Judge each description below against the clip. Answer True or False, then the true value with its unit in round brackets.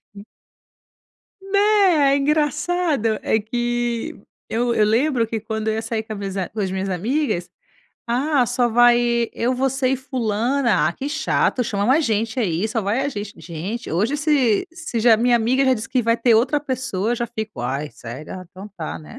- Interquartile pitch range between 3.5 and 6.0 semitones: True (3.9 semitones)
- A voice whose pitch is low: False (235 Hz)